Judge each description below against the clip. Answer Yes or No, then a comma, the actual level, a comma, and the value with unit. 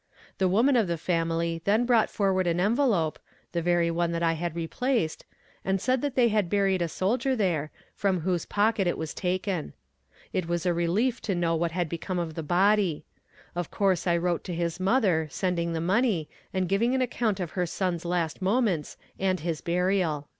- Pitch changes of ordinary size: Yes, average, 3.2 semitones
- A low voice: No, medium, 180 Hz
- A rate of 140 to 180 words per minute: No, average, 190 wpm